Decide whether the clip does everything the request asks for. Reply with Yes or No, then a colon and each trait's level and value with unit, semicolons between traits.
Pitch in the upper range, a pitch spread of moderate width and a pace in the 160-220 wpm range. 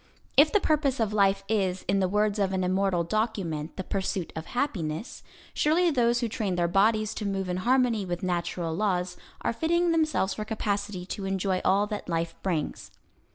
Yes: high, 200 Hz; average, 3.8 semitones; average, 185 wpm